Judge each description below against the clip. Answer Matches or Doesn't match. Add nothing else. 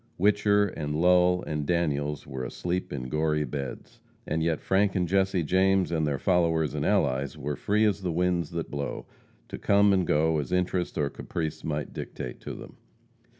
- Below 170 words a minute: Doesn't match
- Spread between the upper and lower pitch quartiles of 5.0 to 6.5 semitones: Doesn't match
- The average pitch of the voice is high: Doesn't match